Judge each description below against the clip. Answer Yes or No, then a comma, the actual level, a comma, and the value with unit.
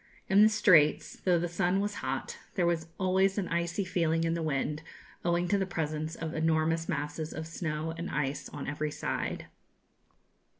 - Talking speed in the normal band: Yes, average, 175 wpm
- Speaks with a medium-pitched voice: Yes, medium, 165 Hz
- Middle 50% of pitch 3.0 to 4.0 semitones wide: No, narrow, 2.6 semitones